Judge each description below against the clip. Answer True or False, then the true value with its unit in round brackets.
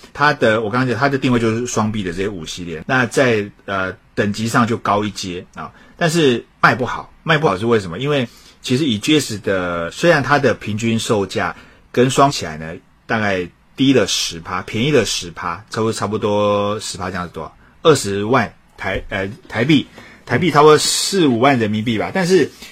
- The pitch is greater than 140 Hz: False (110 Hz)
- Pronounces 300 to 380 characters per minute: False (290 characters per minute)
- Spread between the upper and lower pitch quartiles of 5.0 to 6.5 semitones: True (5.6 semitones)